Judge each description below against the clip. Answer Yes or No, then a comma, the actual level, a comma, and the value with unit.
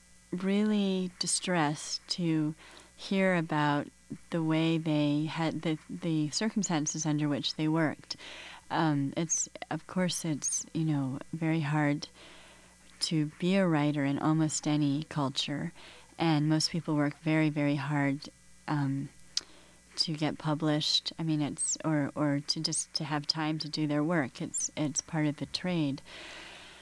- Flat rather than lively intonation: Yes, narrow, 1.8 semitones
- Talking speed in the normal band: Yes, average, 145 wpm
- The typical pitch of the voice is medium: Yes, medium, 155 Hz